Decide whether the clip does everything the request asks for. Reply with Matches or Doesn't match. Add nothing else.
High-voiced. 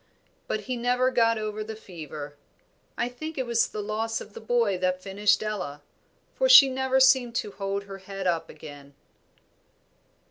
Matches